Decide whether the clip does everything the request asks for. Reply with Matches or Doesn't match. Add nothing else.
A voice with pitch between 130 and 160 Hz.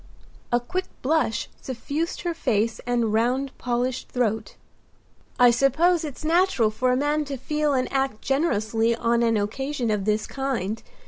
Doesn't match